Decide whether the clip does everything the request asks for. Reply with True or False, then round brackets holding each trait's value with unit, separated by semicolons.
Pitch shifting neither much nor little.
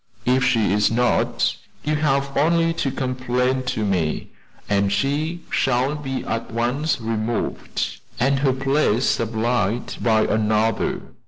True (3.7 semitones)